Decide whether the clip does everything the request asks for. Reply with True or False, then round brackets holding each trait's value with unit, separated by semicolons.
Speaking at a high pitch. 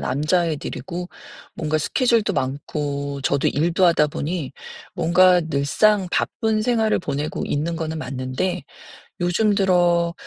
False (170 Hz)